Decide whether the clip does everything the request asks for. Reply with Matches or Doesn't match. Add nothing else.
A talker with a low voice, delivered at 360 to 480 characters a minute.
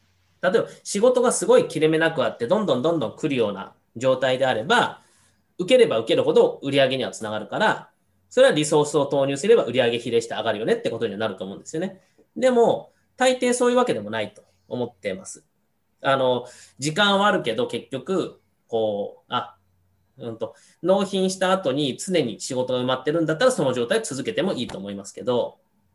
Doesn't match